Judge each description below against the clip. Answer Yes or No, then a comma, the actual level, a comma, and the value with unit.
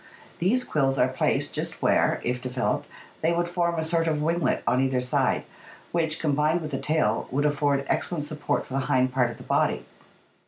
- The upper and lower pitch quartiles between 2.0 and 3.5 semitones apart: No, average, 3.9 semitones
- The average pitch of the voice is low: No, medium, 150 Hz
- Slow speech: No, average, 195 wpm